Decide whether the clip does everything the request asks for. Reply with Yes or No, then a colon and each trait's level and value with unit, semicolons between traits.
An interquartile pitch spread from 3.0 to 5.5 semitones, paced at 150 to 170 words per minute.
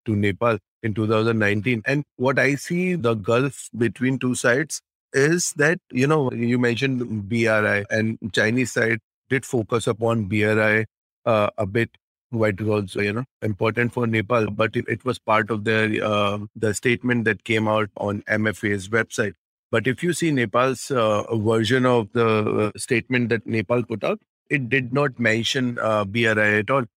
No: narrow, 2.5 semitones; average, 165 wpm